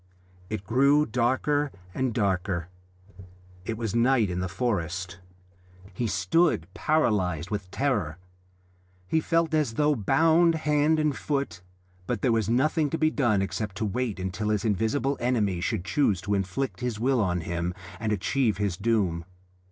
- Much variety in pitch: Yes, wide, 6.4 semitones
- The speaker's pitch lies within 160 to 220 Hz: No, low, 110 Hz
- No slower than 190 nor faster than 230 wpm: No, average, 150 wpm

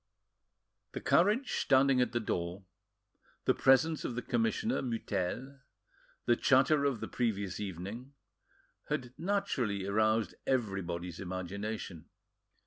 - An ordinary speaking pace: No, slow, 110 wpm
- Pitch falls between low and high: No, low, 115 Hz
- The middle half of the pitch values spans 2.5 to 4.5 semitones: No, wide, 5.4 semitones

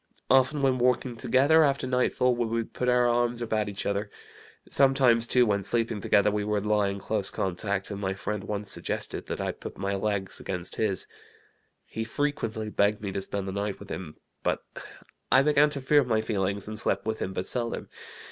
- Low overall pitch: Yes, low, 110 Hz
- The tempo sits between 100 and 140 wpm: No, average, 200 wpm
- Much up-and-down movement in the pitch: No, average, 3.8 semitones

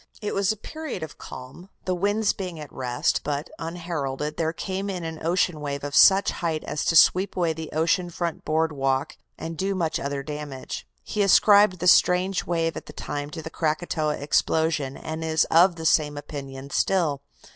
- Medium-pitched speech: Yes, medium, 160 Hz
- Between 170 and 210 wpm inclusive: Yes, average, 185 wpm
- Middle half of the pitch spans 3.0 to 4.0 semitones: Yes, average, 3.5 semitones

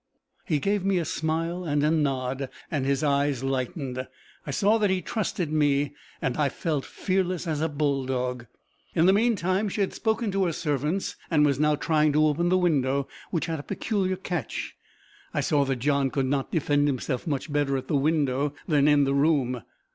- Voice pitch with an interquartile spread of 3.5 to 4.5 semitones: Yes, average, 4.0 semitones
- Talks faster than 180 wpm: Yes, average, 195 wpm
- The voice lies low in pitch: No, medium, 150 Hz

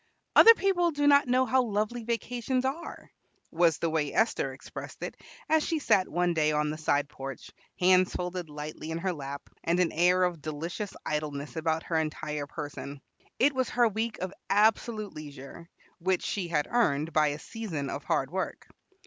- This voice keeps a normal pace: Yes, average, 180 wpm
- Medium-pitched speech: Yes, medium, 175 Hz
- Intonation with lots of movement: Yes, wide, 6.9 semitones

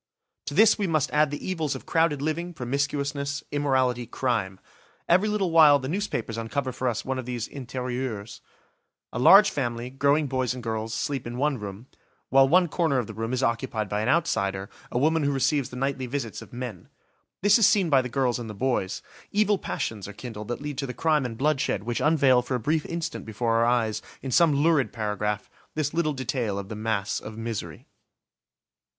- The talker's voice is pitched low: Yes, low, 130 Hz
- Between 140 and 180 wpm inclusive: No, average, 200 wpm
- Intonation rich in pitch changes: No, average, 4.6 semitones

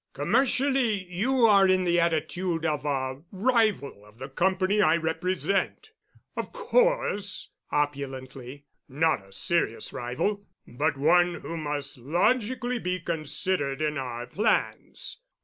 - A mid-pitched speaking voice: Yes, medium, 170 Hz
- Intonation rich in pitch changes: Yes, wide, 6.3 semitones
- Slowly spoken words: Yes, slow, 115 wpm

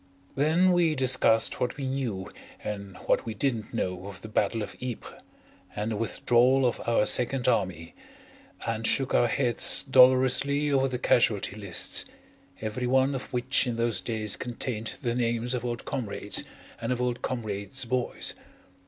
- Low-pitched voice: Yes, low, 120 Hz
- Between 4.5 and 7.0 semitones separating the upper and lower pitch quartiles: No, average, 3.1 semitones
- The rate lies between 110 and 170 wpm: Yes, average, 160 wpm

